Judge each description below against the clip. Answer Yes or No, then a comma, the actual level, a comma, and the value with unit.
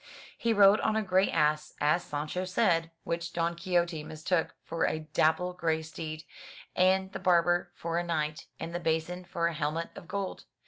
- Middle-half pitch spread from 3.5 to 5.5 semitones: No, narrow, 2.4 semitones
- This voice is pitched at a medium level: Yes, medium, 170 Hz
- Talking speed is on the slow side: No, average, 180 wpm